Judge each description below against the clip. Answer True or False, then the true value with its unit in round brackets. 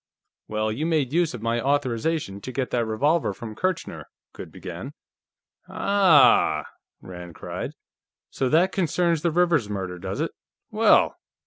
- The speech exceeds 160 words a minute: False (145 wpm)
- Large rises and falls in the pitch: True (7.2 semitones)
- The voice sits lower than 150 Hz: True (135 Hz)